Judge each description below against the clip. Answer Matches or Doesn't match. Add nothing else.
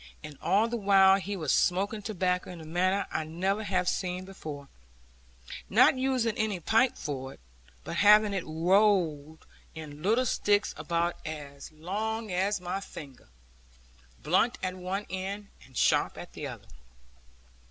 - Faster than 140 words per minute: Matches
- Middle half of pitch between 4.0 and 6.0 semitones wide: Matches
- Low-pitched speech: Doesn't match